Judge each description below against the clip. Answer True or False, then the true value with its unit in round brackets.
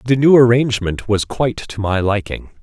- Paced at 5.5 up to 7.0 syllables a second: False (5.2 syllables/s)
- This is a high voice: False (115 Hz)